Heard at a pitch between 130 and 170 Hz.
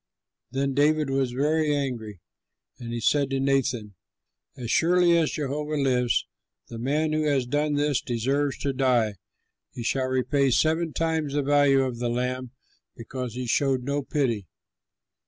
Yes: low, 135 Hz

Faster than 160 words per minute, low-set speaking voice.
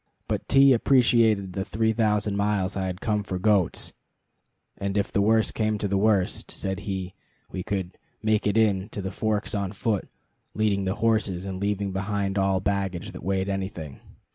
Yes: average, 180 wpm; low, 100 Hz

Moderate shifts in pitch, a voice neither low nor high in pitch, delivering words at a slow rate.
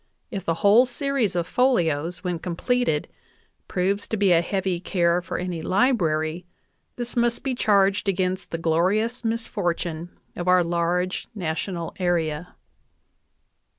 Yes: average, 3.8 semitones; medium, 180 Hz; slow, 130 wpm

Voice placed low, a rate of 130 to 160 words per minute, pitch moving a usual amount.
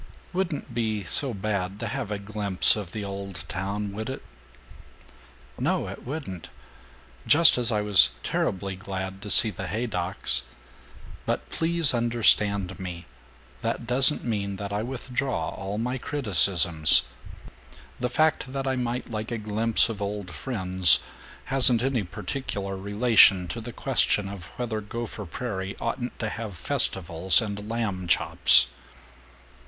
Yes: low, 105 Hz; average, 140 wpm; average, 3.9 semitones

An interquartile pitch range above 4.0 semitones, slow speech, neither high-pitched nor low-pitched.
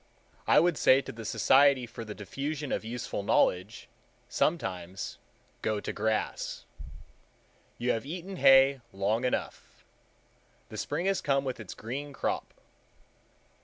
No: average, 4.5 semitones; slow, 130 wpm; low, 125 Hz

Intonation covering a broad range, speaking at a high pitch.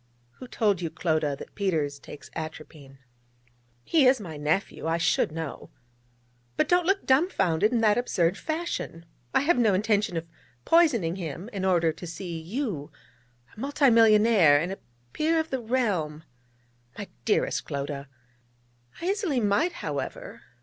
Yes: wide, 7.8 semitones; high, 200 Hz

